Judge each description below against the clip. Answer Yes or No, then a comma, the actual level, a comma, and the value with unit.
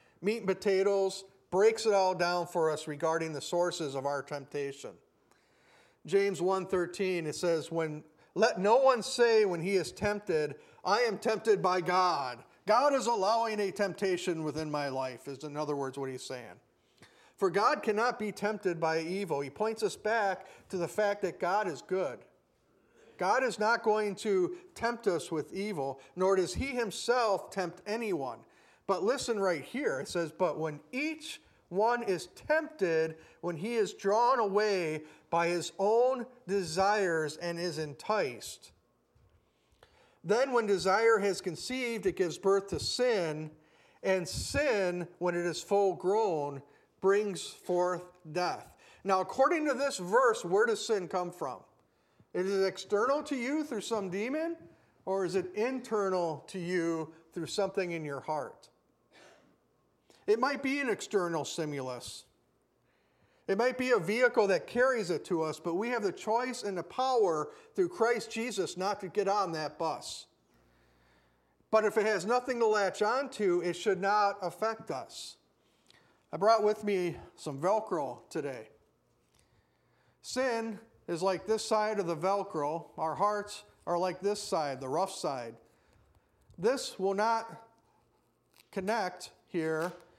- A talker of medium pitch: No, high, 195 Hz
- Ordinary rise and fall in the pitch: Yes, average, 4.8 semitones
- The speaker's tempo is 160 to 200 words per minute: No, average, 150 wpm